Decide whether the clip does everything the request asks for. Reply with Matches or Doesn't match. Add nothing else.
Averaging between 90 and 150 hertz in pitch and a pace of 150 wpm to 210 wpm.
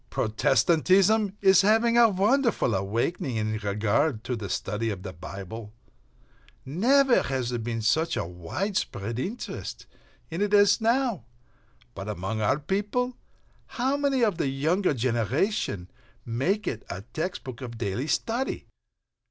Doesn't match